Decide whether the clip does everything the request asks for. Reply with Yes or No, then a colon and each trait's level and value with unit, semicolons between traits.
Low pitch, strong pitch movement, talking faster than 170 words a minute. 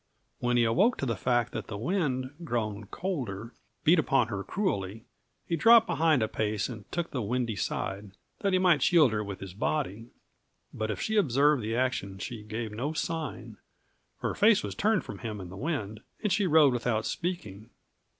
Yes: low, 120 Hz; wide, 7.3 semitones; average, 190 wpm